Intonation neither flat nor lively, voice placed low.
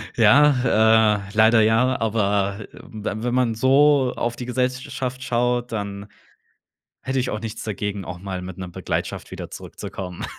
Yes: average, 3.5 semitones; low, 110 Hz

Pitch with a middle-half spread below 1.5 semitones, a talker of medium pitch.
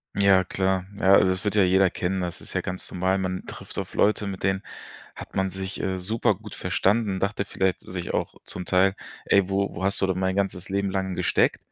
No: narrow, 1.0 semitones; very low, 95 Hz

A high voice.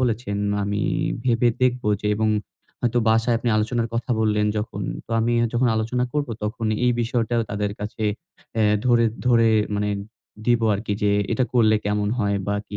No: low, 115 Hz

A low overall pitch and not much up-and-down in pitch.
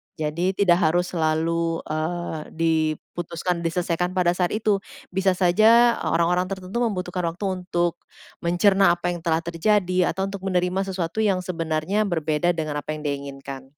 No: medium, 175 Hz; narrow, 2.3 semitones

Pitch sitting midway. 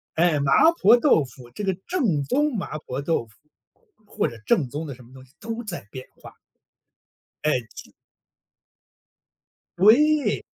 Yes: medium, 165 Hz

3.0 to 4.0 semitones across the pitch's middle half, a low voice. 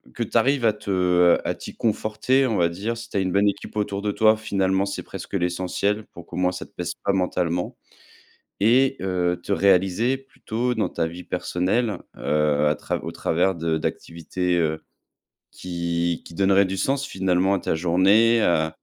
Yes: average, 3.6 semitones; very low, 95 Hz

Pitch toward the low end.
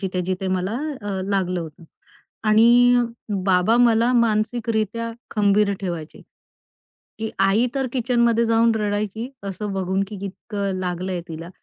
No: high, 205 Hz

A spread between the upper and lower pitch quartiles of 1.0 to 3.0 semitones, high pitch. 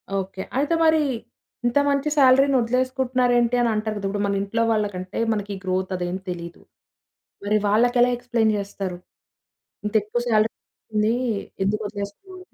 No: average, 3.6 semitones; high, 220 Hz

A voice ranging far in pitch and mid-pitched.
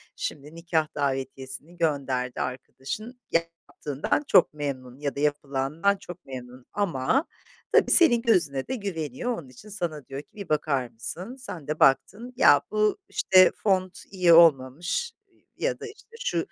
Yes: wide, 6.7 semitones; medium, 155 Hz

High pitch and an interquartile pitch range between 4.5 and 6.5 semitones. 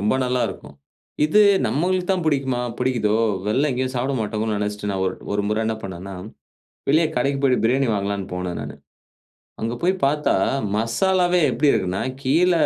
No: low, 125 Hz; wide, 5.5 semitones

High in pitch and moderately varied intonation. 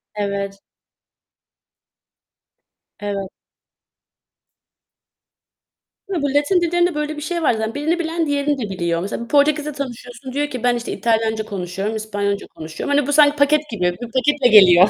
No: high, 245 Hz; wide, 6.4 semitones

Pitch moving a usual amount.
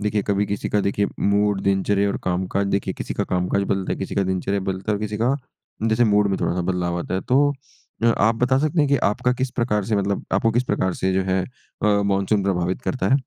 No: narrow, 1.9 semitones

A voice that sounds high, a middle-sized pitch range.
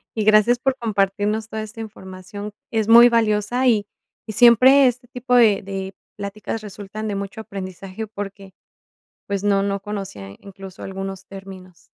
No: high, 205 Hz; narrow, 2.3 semitones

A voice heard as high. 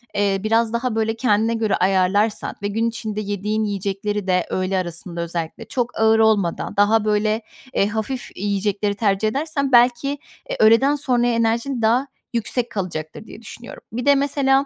Yes: high, 220 Hz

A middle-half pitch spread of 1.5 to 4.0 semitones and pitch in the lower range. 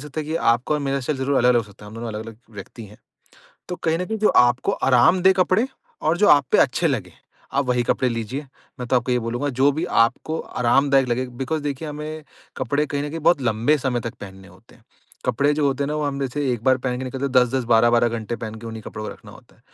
Yes: average, 3.7 semitones; low, 130 Hz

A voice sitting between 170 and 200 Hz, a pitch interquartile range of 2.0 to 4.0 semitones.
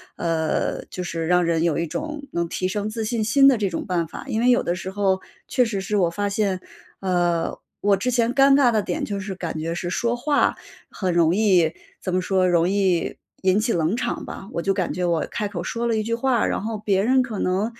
No: high, 195 Hz; average, 4.5 semitones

